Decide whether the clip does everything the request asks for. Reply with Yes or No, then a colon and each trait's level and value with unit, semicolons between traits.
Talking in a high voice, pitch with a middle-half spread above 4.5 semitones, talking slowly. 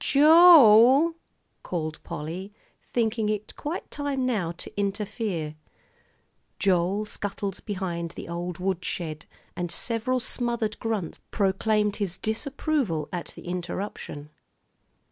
Yes: high, 205 Hz; average, 5.0 semitones; slow, 105 wpm